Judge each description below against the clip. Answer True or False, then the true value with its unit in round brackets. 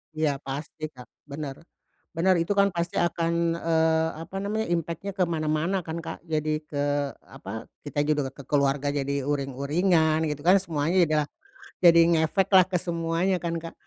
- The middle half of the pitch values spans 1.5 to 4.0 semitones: True (2.8 semitones)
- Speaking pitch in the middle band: True (160 Hz)